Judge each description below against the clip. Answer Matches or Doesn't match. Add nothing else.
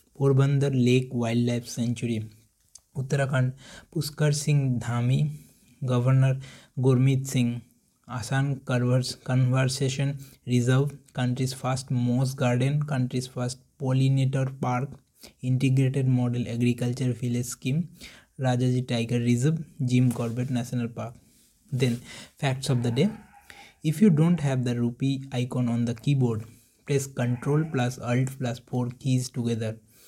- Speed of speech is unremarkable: Doesn't match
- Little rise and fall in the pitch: Matches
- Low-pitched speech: Matches